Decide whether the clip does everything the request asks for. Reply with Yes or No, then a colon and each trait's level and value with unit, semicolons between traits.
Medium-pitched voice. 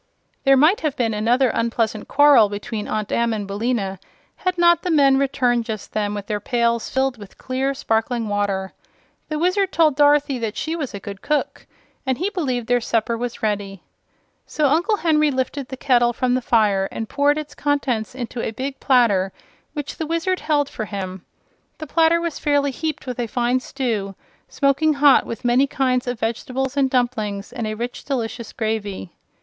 No: very high, 250 Hz